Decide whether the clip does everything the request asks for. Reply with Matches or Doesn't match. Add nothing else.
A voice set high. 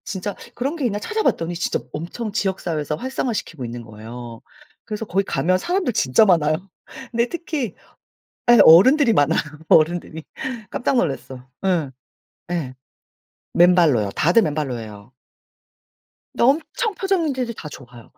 Doesn't match